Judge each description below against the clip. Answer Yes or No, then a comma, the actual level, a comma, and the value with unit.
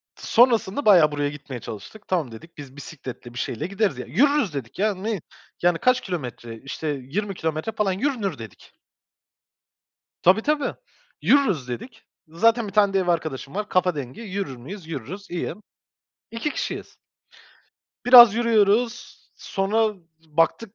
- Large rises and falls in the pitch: Yes, wide, 7.1 semitones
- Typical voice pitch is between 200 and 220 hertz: No, medium, 185 Hz